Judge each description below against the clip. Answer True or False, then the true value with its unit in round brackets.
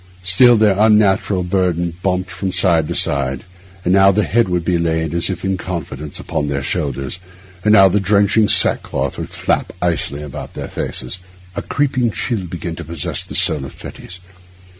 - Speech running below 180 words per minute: False (185 wpm)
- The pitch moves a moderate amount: True (3.4 semitones)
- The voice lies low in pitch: True (90 Hz)